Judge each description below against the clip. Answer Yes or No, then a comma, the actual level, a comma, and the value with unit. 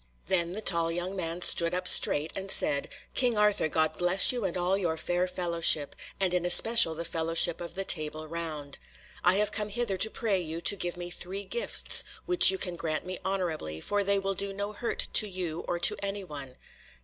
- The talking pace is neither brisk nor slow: No, fast, 210 wpm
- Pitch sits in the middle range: Yes, medium, 180 Hz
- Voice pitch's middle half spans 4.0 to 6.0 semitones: No, average, 3.0 semitones